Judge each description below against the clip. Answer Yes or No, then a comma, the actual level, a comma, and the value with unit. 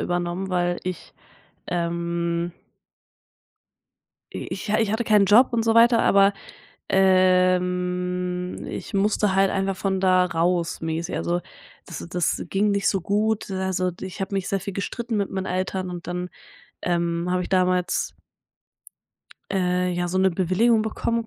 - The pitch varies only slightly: Yes, narrow, 1.9 semitones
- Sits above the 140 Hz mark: Yes, medium, 185 Hz